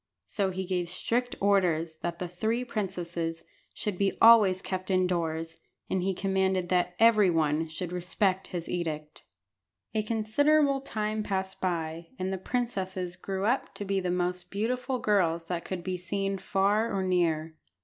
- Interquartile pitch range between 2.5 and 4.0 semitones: Yes, average, 2.8 semitones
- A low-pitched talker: No, medium, 185 Hz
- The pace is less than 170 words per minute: Yes, average, 160 wpm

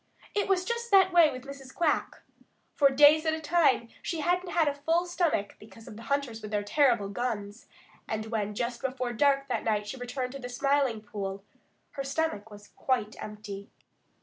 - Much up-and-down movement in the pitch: Yes, wide, 5.9 semitones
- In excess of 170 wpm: Yes, average, 190 wpm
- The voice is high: Yes, very high, 260 Hz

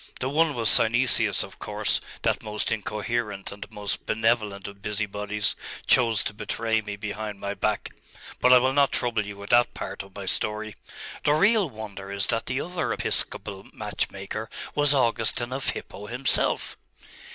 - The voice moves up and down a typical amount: Yes, average, 3.3 semitones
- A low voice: Yes, low, 110 Hz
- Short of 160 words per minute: No, average, 165 wpm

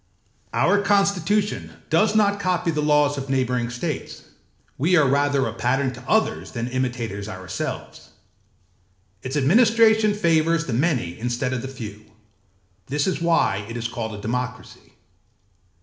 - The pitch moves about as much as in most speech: No, wide, 6.6 semitones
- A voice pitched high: No, medium, 140 Hz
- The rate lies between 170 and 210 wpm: No, average, 140 wpm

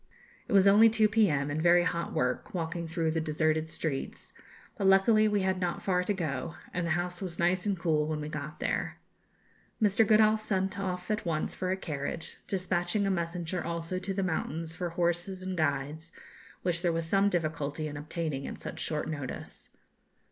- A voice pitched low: No, medium, 175 Hz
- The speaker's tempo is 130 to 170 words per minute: No, average, 190 wpm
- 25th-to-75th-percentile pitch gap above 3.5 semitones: No, average, 3.2 semitones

